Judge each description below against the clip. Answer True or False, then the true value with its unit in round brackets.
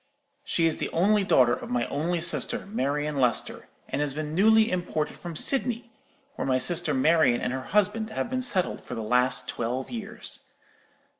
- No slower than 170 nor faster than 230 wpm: True (175 wpm)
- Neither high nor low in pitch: True (165 Hz)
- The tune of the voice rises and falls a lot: True (8.2 semitones)